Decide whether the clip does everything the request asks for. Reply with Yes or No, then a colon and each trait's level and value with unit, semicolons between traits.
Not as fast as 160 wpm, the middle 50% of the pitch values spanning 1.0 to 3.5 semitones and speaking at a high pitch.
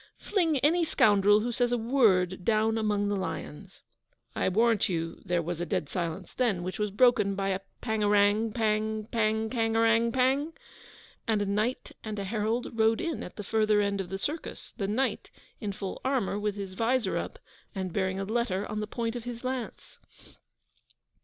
No: average, 180 wpm; average, 3.0 semitones; high, 215 Hz